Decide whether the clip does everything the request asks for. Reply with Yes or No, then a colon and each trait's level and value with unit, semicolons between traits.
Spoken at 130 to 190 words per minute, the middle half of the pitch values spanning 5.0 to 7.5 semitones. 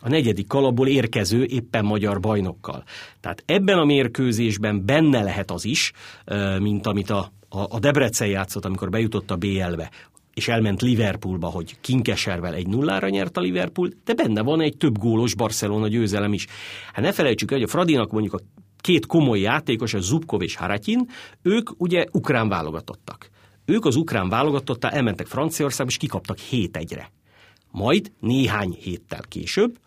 Yes: fast, 155 wpm; wide, 5.5 semitones